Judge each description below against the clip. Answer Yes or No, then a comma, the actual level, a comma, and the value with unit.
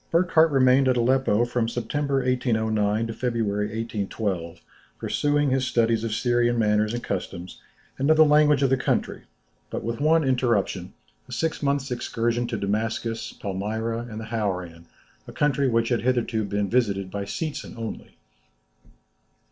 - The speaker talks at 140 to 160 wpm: Yes, average, 155 wpm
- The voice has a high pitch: No, low, 115 Hz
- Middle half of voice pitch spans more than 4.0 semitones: No, average, 3.7 semitones